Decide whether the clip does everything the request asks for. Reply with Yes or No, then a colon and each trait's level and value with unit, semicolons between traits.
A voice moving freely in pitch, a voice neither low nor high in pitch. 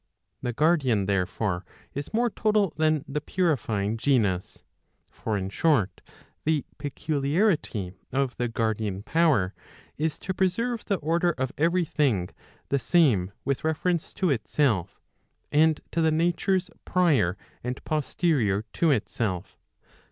Yes: wide, 7.3 semitones; medium, 145 Hz